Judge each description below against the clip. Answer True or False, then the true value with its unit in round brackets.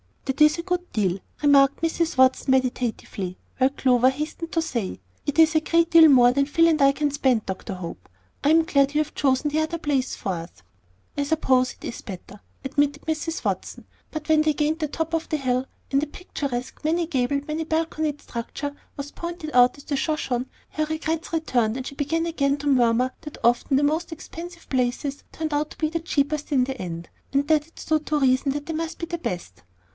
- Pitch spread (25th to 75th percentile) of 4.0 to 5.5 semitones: False (3.6 semitones)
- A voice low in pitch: False (290 Hz)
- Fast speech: True (210 wpm)